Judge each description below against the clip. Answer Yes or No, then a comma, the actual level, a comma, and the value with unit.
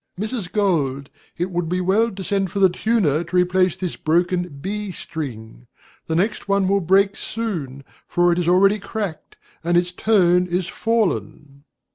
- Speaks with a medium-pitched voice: Yes, medium, 180 Hz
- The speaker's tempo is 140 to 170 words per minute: Yes, average, 165 wpm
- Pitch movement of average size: Yes, average, 3.0 semitones